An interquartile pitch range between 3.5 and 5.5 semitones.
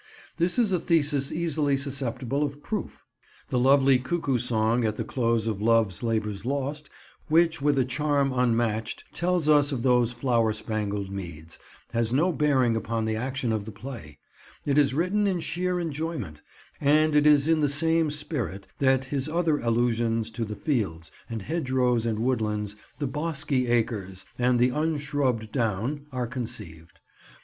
Yes: average, 4.7 semitones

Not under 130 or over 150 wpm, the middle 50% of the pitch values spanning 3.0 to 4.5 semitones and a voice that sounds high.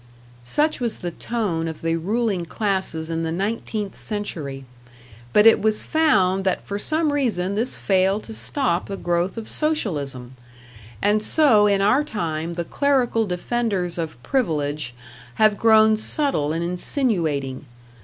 No: average, 145 wpm; wide, 5.4 semitones; high, 200 Hz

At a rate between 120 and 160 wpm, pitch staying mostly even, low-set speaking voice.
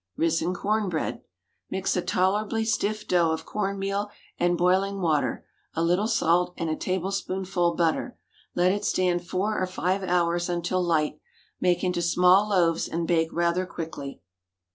No: average, 155 wpm; narrow, 2.2 semitones; medium, 180 Hz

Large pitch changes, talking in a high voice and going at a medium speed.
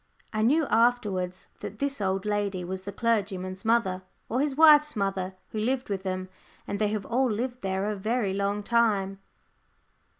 No: average, 3.6 semitones; high, 205 Hz; average, 170 wpm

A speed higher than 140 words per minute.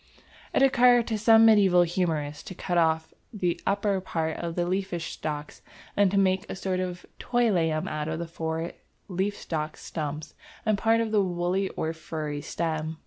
Yes: average, 180 wpm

